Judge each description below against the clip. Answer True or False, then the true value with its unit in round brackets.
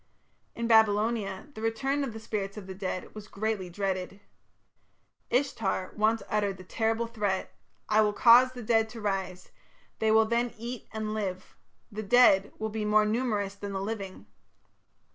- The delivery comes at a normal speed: True (160 wpm)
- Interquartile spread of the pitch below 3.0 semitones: True (2.4 semitones)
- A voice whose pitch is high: True (215 Hz)